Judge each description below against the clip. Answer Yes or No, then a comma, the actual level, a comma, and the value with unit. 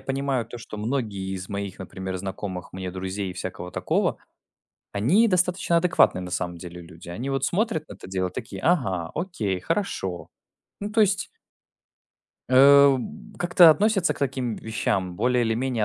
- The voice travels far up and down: Yes, wide, 8.6 semitones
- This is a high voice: No, low, 115 Hz